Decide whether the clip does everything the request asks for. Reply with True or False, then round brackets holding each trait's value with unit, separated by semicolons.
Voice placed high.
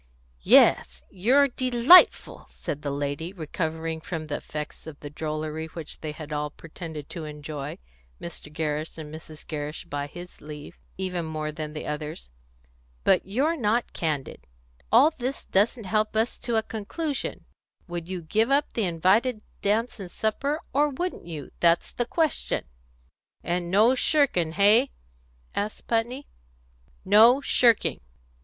False (175 Hz)